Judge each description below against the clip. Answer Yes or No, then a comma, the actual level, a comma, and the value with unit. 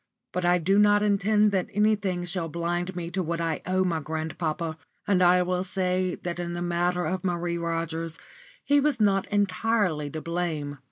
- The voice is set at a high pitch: No, medium, 180 Hz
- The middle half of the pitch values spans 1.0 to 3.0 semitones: Yes, narrow, 2.5 semitones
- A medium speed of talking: Yes, average, 180 wpm